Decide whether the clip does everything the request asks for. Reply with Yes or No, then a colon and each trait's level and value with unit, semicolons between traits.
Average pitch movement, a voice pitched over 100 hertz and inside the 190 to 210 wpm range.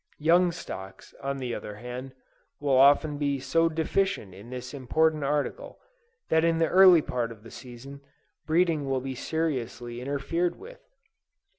No: average, 4.5 semitones; medium, 140 Hz; average, 150 wpm